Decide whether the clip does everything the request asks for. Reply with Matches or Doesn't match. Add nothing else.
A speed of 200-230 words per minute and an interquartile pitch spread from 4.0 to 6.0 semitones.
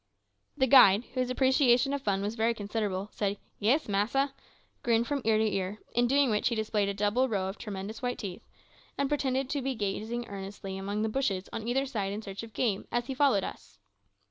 Matches